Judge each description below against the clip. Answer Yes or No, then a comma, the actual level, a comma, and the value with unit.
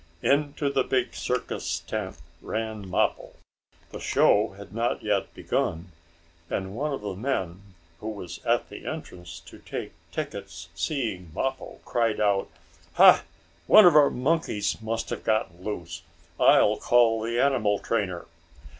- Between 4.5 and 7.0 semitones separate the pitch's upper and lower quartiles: Yes, average, 5.1 semitones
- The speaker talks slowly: No, average, 145 wpm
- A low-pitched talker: Yes, low, 110 Hz